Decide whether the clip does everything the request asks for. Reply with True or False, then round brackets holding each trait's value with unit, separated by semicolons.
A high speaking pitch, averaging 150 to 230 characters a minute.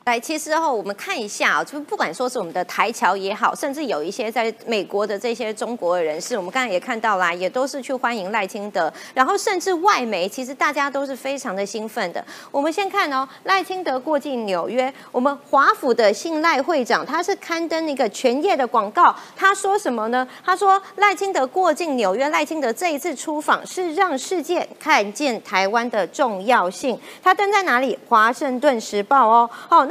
False (265 Hz; 305 characters per minute)